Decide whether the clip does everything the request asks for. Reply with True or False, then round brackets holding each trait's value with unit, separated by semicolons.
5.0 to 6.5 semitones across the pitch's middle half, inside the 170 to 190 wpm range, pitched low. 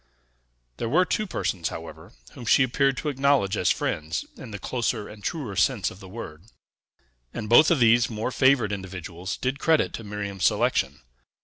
True (5.5 semitones; 175 wpm; 110 Hz)